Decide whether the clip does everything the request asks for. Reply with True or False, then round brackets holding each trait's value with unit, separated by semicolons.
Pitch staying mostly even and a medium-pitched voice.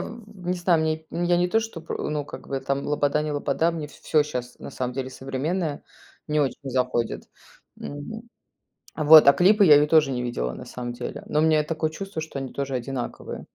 False (3.5 semitones; 150 Hz)